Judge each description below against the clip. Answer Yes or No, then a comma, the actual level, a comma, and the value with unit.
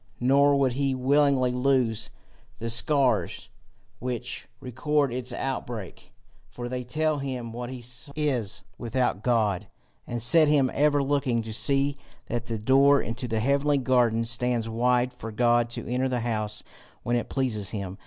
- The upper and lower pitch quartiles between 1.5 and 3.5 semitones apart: Yes, average, 2.9 semitones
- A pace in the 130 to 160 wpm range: Yes, average, 155 wpm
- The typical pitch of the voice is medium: No, low, 125 Hz